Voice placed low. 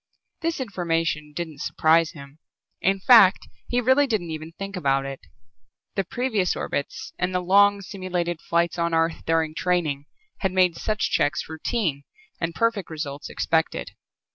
No: medium, 170 Hz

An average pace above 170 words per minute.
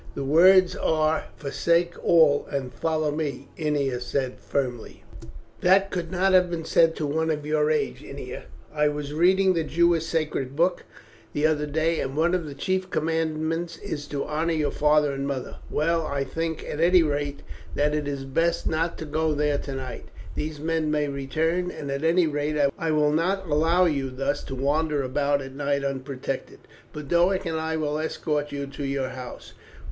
Yes: average, 180 wpm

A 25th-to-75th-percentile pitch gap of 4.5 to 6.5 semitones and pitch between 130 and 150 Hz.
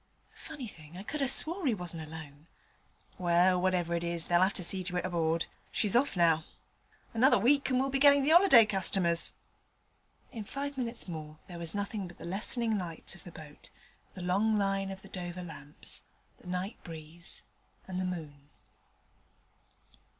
No: average, 4.8 semitones; medium, 185 Hz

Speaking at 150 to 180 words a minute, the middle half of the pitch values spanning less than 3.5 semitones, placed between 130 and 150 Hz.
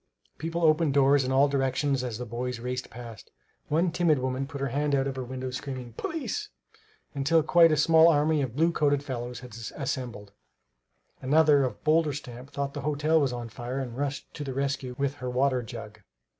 No: average, 195 wpm; average, 2.8 semitones; low, 135 Hz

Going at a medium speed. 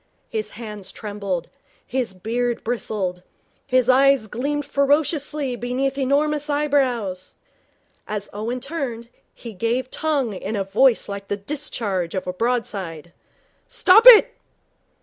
No: slow, 120 wpm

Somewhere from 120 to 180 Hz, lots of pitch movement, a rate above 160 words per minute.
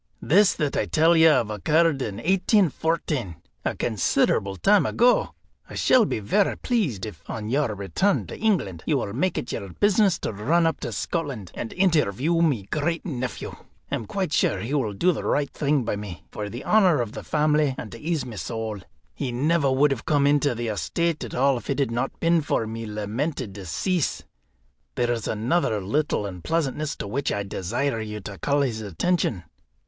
Yes: low, 135 Hz; wide, 7.3 semitones; average, 190 wpm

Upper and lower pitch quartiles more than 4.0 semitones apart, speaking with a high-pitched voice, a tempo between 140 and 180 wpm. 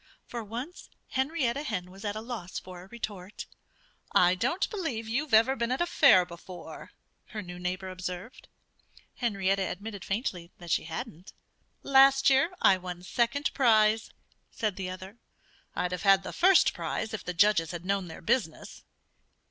Yes: average, 4.9 semitones; high, 205 Hz; average, 160 wpm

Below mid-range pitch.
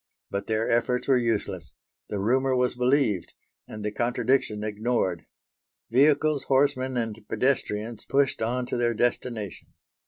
Yes: low, 120 Hz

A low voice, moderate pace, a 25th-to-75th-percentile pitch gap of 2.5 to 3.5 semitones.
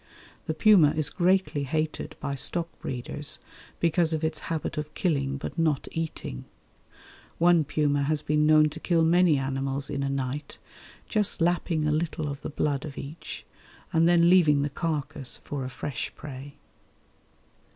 No: medium, 150 Hz; average, 160 wpm; average, 2.8 semitones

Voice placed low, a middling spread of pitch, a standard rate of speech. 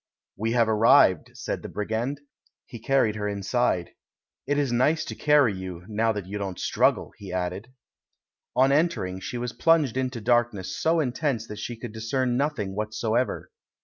Yes: low, 115 Hz; average, 4.1 semitones; average, 170 wpm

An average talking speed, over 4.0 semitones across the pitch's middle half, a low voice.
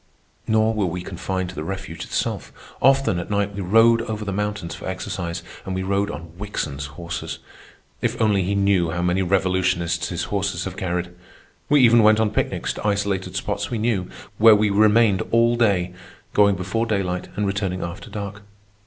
No: average, 180 wpm; average, 2.8 semitones; low, 100 Hz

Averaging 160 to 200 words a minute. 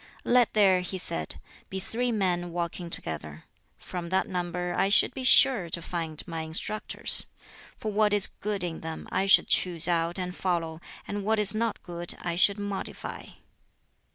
Yes: average, 170 wpm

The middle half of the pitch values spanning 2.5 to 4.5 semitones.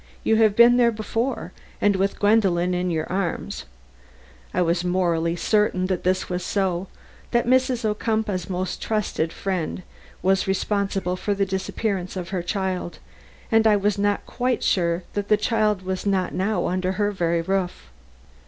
Yes: average, 2.8 semitones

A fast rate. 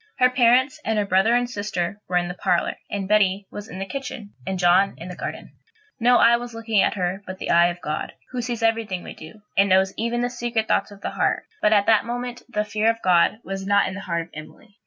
Yes: fast, 255 wpm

